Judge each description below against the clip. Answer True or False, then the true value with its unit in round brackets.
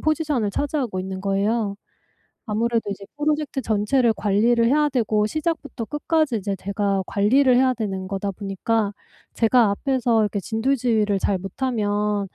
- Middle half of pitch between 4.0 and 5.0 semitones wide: True (4.4 semitones)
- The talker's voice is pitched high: True (220 Hz)